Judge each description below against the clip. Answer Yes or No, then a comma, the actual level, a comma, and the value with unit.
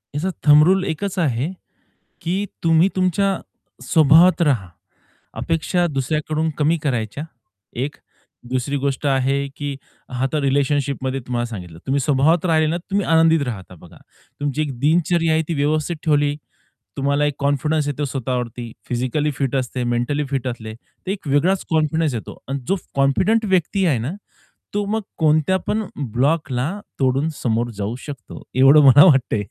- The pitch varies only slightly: No, average, 3.8 semitones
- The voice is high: No, medium, 145 Hz